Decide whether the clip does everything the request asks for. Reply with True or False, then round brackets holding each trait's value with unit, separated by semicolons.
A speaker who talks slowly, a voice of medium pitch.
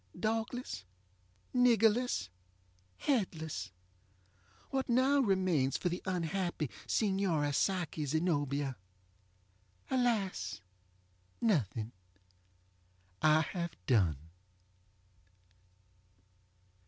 True (55 wpm; 170 Hz)